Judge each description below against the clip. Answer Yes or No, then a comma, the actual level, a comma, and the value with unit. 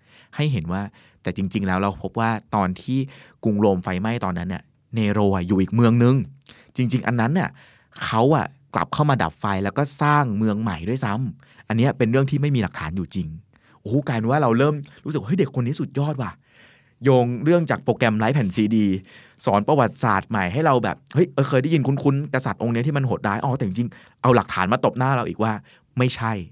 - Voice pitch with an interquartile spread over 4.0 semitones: Yes, average, 5.0 semitones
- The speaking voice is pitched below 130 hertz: Yes, low, 120 Hz